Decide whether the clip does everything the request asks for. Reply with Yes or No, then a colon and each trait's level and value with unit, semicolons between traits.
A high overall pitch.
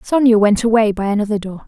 Yes: high, 215 Hz